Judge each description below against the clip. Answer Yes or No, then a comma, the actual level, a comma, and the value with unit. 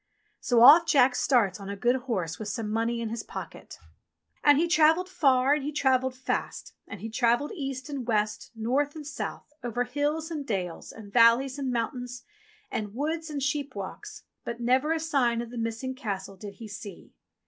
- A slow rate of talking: No, average, 185 wpm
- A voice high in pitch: Yes, very high, 250 Hz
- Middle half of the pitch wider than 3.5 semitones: Yes, average, 4.3 semitones